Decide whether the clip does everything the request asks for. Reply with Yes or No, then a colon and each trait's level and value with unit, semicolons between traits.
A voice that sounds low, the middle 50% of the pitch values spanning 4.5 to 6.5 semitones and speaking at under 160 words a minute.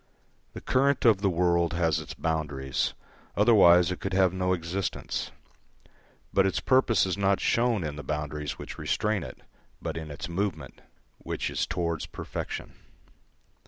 No: very low, 90 Hz; average, 3.4 semitones; average, 150 wpm